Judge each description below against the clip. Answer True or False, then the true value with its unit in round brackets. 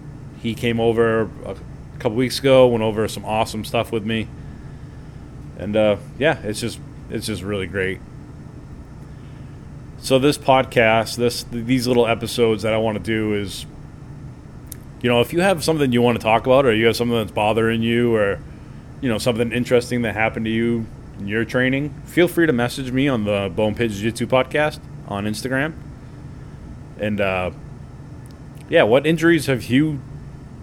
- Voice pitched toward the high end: False (120 Hz)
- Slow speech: False (170 wpm)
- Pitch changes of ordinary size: True (3.4 semitones)